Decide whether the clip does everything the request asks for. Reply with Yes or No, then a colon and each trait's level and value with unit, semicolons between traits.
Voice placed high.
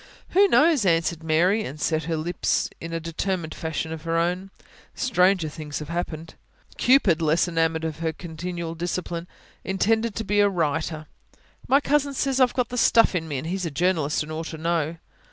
No: medium, 170 Hz